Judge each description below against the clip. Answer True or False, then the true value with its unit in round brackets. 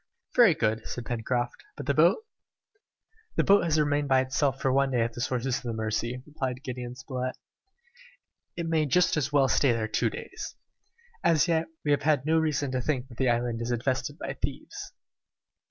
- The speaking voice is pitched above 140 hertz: False (130 Hz)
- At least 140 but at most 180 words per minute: False (190 wpm)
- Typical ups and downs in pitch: True (3.6 semitones)